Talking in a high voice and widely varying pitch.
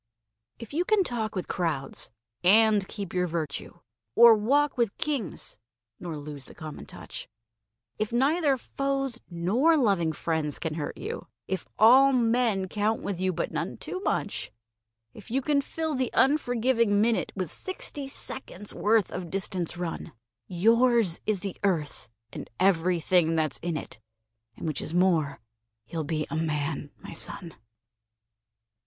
Yes: high, 200 Hz; wide, 6.8 semitones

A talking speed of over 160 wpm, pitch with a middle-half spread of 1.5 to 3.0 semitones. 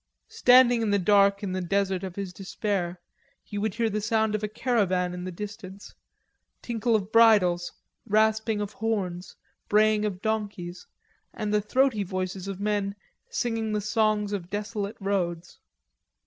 No: average, 155 wpm; narrow, 2.6 semitones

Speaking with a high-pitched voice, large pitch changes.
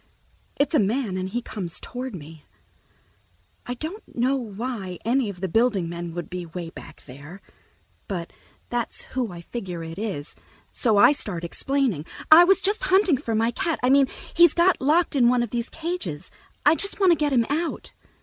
Yes: high, 235 Hz; wide, 7.7 semitones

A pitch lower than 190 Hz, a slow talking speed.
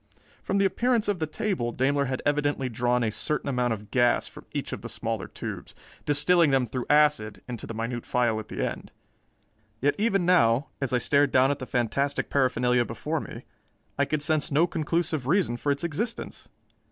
No: medium, 140 Hz; average, 190 wpm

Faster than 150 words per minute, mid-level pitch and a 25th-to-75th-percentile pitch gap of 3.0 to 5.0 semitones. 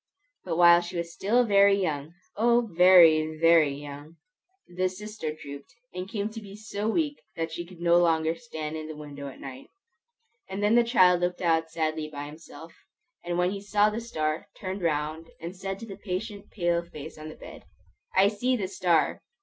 Yes: average, 190 wpm; medium, 175 Hz; average, 4.2 semitones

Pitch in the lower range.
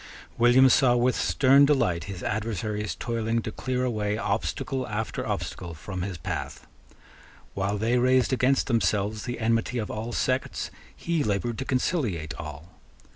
Yes: low, 115 Hz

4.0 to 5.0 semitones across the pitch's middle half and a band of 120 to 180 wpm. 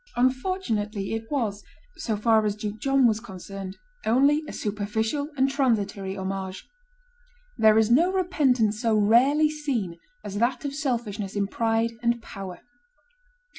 Yes: average, 4.4 semitones; slow, 135 wpm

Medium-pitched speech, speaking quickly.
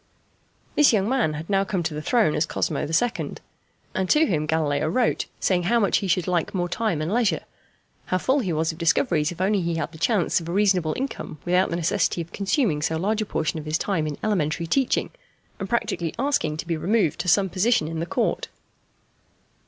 Yes: medium, 175 Hz; fast, 215 wpm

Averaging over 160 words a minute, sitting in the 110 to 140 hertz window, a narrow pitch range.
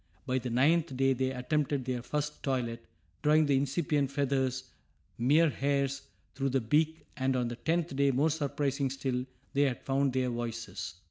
Yes: average, 170 wpm; low, 135 Hz; narrow, 2.2 semitones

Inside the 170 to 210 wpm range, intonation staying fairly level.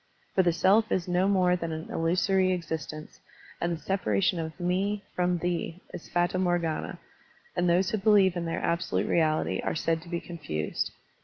Yes: average, 175 wpm; narrow, 2.1 semitones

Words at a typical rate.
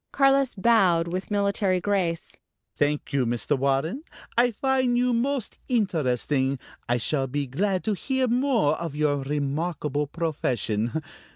No: slow, 130 wpm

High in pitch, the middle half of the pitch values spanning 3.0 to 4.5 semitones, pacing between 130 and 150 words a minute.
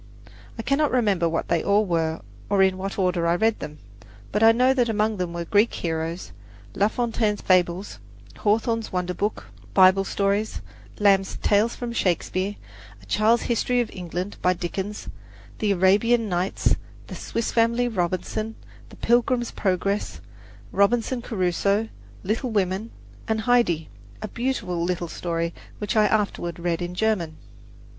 Yes: high, 200 Hz; average, 3.9 semitones; average, 145 wpm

